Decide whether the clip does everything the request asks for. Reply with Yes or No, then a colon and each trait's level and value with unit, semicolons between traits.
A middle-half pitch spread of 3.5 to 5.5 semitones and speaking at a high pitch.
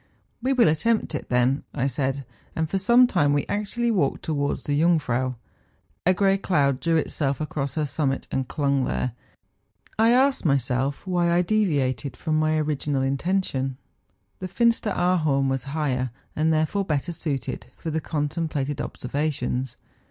No: average, 4.6 semitones; medium, 150 Hz